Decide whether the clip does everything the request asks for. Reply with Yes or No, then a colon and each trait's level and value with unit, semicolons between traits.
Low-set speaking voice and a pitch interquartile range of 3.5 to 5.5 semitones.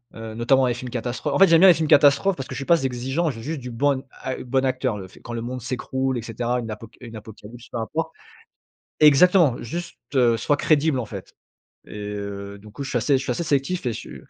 Yes: low, 130 Hz; average, 3.8 semitones